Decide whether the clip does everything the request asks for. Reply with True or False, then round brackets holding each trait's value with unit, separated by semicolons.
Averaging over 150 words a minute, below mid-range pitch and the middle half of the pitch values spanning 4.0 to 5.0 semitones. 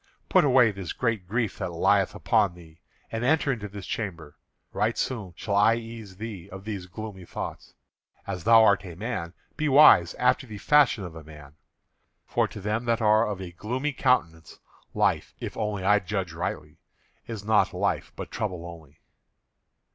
True (175 wpm; 105 Hz; 4.3 semitones)